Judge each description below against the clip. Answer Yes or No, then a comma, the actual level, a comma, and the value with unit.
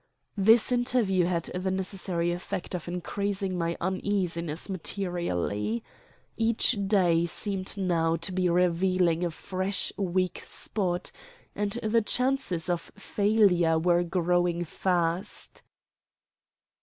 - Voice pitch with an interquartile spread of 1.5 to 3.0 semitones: Yes, narrow, 2.4 semitones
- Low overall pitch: No, medium, 180 Hz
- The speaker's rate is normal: No, slow, 105 wpm